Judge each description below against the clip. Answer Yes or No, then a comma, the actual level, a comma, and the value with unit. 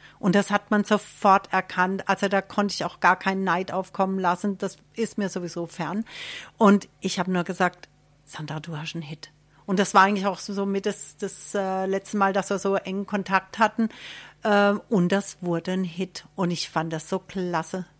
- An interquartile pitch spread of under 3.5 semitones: Yes, narrow, 2.4 semitones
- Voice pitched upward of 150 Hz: Yes, high, 190 Hz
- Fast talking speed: Yes, fast, 195 wpm